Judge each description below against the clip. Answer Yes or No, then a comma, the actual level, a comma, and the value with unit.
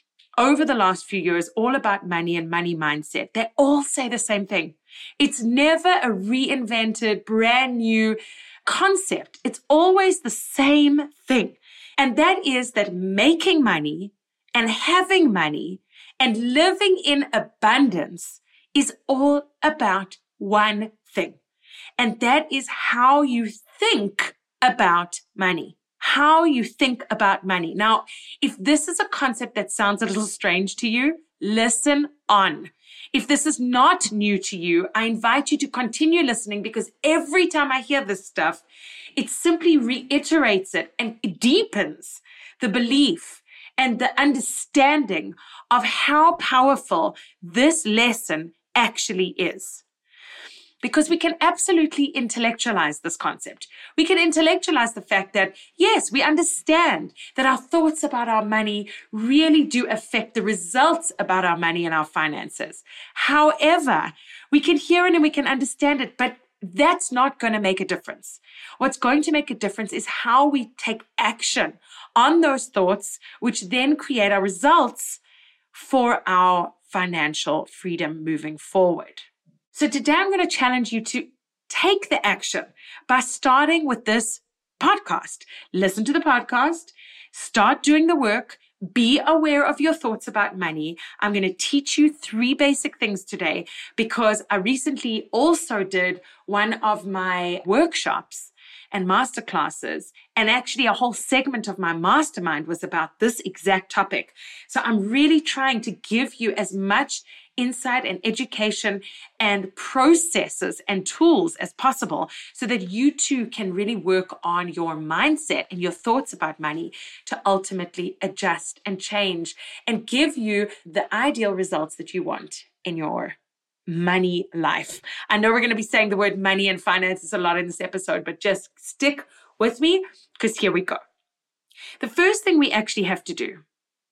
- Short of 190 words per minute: Yes, average, 150 wpm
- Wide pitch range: Yes, wide, 6.6 semitones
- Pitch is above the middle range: Yes, high, 240 Hz